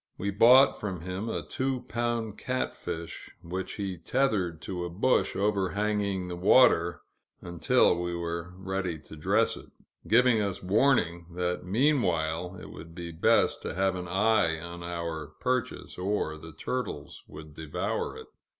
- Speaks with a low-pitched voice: Yes, very low, 90 Hz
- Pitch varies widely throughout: No, average, 4.0 semitones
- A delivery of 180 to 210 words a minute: No, average, 150 wpm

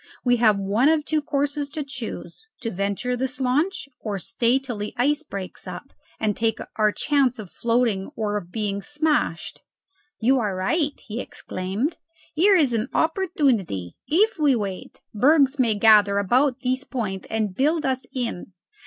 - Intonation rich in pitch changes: Yes, wide, 5.7 semitones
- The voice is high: Yes, high, 245 Hz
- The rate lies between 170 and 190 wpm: No, average, 160 wpm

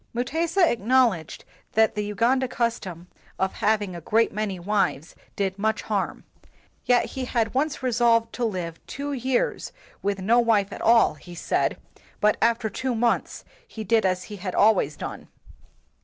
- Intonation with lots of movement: No, average, 3.7 semitones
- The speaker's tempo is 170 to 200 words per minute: No, average, 155 wpm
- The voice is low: No, high, 220 Hz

